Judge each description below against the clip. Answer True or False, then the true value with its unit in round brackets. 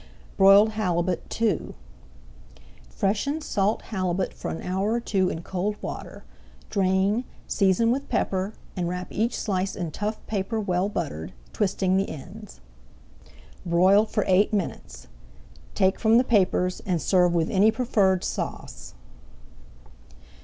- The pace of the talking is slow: True (130 wpm)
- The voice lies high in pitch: True (195 Hz)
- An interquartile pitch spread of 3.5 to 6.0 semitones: False (2.7 semitones)